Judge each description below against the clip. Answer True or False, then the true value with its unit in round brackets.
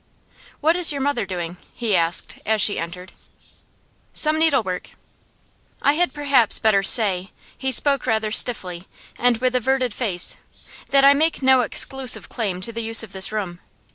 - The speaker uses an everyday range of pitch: False (5.8 semitones)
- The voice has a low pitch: False (230 Hz)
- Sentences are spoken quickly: False (160 wpm)